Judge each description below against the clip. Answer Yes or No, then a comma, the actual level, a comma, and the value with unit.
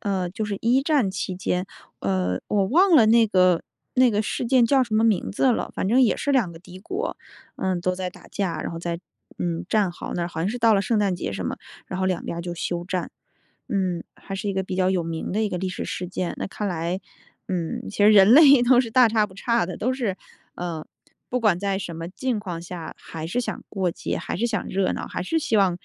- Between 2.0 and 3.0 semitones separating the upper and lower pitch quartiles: No, average, 4.3 semitones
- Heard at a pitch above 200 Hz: No, high, 190 Hz